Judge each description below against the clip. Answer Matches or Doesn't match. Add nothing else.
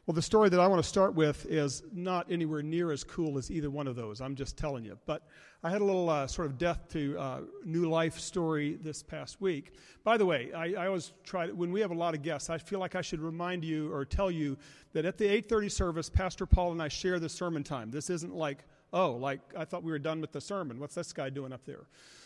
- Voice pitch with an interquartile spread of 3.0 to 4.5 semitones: Matches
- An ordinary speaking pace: Doesn't match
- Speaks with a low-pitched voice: Doesn't match